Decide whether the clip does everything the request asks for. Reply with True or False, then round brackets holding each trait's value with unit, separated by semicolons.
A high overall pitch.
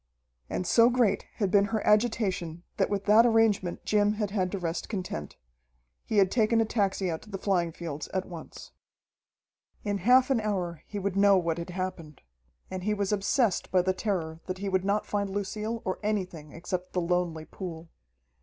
True (195 Hz)